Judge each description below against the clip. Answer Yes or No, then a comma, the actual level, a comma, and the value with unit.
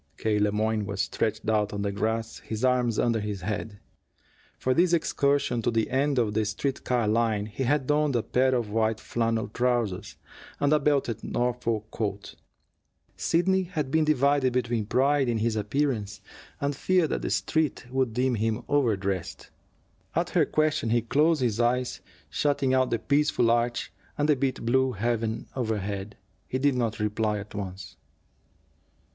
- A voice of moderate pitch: No, low, 120 Hz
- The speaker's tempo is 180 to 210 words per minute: No, average, 170 wpm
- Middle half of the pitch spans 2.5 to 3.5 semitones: No, average, 4.2 semitones